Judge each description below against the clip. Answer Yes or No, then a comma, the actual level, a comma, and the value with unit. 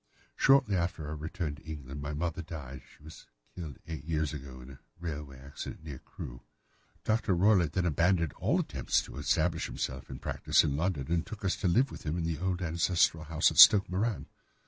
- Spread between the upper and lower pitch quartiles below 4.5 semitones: Yes, average, 3.4 semitones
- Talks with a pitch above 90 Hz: No, very low, 80 Hz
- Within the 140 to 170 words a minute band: No, average, 195 wpm